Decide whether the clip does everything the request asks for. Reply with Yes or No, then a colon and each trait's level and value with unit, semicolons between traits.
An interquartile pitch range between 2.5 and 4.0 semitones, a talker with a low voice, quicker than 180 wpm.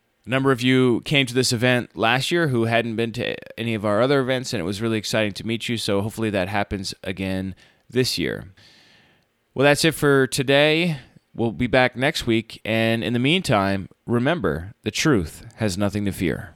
Yes: average, 3.7 semitones; low, 115 Hz; average, 200 wpm